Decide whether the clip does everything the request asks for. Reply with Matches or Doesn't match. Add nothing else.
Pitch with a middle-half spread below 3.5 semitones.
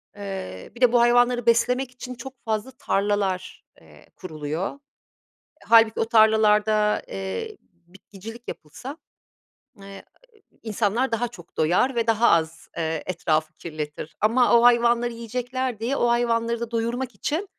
Doesn't match